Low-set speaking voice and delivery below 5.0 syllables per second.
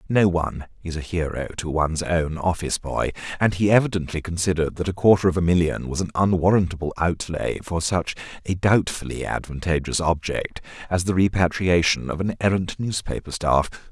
No: very low, 85 Hz; 5.5 syllables/s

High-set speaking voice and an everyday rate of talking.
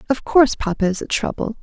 No: high, 235 Hz; fast, 220 wpm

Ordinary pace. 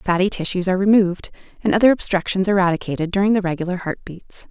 Yes: average, 175 wpm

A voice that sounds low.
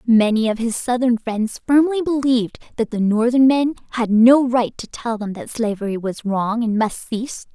No: high, 235 Hz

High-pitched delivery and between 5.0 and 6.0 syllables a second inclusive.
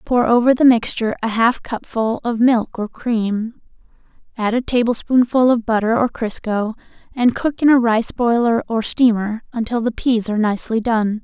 No: high, 230 Hz; 4.8 syllables/s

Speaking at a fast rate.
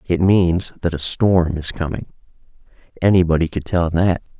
No: average, 150 wpm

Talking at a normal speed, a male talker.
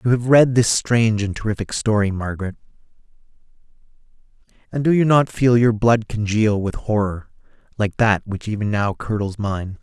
Yes: average, 160 wpm; male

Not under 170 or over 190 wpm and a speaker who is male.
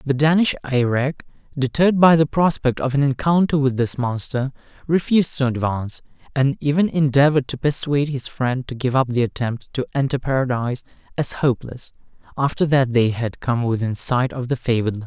Yes: average, 175 wpm; male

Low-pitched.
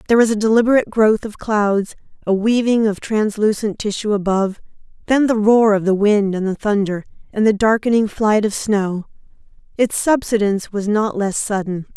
No: high, 210 Hz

